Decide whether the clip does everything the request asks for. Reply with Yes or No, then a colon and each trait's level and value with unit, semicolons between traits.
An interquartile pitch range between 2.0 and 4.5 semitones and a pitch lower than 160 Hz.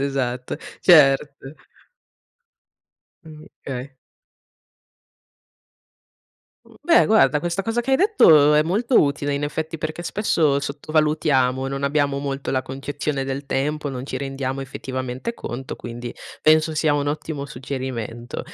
Yes: narrow, 2.6 semitones; medium, 140 Hz